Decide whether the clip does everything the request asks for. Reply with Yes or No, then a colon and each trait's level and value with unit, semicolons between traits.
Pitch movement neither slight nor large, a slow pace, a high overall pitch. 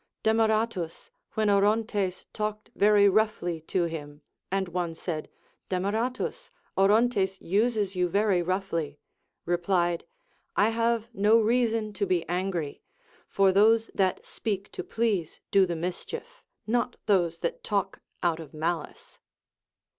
Yes: average, 3.9 semitones; slow, 130 wpm; high, 195 Hz